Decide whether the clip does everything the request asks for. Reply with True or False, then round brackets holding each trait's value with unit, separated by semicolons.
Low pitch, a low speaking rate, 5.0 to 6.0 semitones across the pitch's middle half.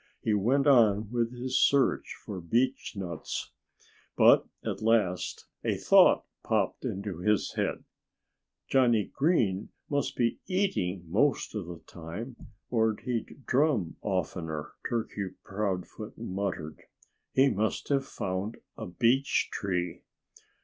True (105 Hz; 115 wpm; 5.3 semitones)